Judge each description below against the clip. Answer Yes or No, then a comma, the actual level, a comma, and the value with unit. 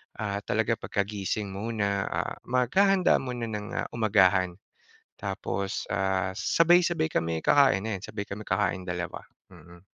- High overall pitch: No, low, 105 Hz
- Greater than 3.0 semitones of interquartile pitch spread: Yes, average, 3.4 semitones